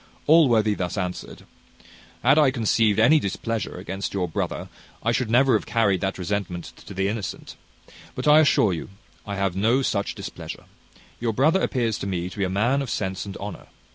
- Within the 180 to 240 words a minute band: Yes, average, 185 wpm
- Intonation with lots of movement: No, average, 4.1 semitones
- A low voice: Yes, low, 105 Hz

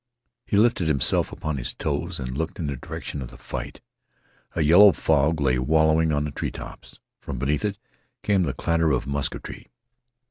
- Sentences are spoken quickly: No, average, 175 wpm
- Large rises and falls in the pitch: No, average, 3.1 semitones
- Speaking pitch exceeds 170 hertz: No, very low, 75 Hz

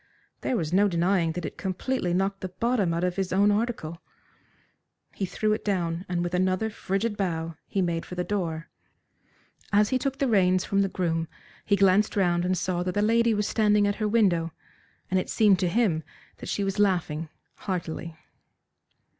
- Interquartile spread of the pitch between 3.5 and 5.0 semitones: No, average, 3.0 semitones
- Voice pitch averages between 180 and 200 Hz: Yes, medium, 185 Hz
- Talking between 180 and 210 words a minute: Yes, average, 190 wpm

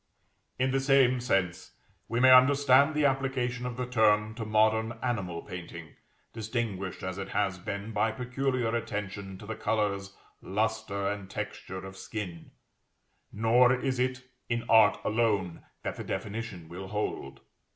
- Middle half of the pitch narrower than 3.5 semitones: No, average, 4.2 semitones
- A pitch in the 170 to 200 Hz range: No, low, 110 Hz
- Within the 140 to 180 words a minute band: Yes, average, 145 wpm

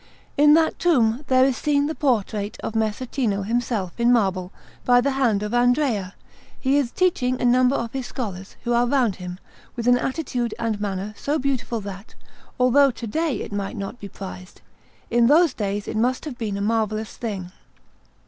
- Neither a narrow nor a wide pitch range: Yes, average, 4.2 semitones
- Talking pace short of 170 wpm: No, average, 185 wpm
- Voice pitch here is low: No, high, 235 Hz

